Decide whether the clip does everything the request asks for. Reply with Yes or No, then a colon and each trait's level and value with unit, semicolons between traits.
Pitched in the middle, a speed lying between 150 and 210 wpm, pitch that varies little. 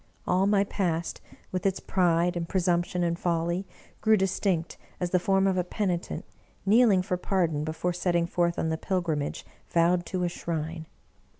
Yes: medium, 175 Hz; average, 165 wpm; narrow, 1.9 semitones